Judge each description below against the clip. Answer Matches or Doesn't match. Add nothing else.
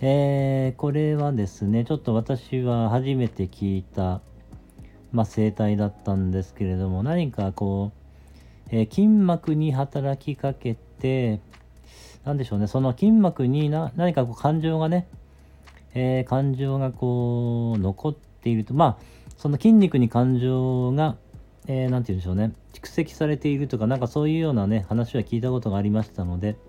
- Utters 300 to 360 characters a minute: Matches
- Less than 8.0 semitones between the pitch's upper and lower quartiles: Matches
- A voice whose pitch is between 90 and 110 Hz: Doesn't match